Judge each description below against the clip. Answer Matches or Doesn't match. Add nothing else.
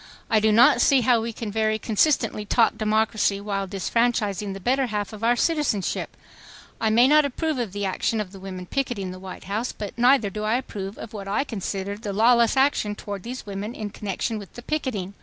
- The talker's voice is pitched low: Doesn't match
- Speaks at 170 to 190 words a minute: Doesn't match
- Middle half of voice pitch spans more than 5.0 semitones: Doesn't match